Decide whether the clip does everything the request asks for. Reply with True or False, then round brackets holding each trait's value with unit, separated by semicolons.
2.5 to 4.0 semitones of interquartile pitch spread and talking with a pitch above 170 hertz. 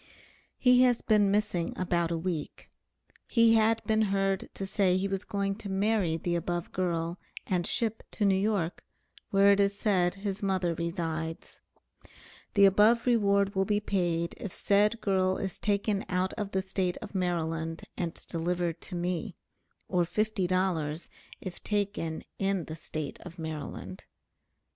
True (2.9 semitones; 190 Hz)